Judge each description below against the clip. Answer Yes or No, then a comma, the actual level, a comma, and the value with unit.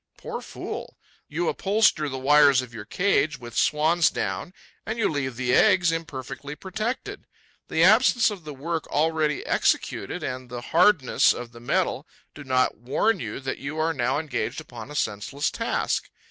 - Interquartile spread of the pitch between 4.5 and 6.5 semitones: Yes, average, 4.9 semitones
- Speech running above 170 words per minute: No, average, 165 wpm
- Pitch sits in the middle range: Yes, medium, 150 Hz